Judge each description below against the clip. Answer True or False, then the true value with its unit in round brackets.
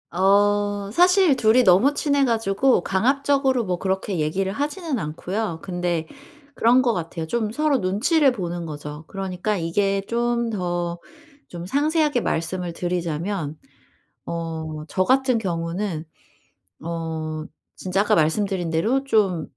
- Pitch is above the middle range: True (195 Hz)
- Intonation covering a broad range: True (5.9 semitones)